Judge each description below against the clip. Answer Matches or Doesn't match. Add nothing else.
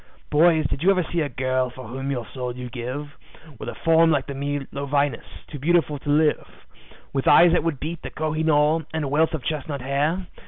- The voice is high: Doesn't match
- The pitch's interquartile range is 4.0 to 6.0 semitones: Doesn't match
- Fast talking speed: Matches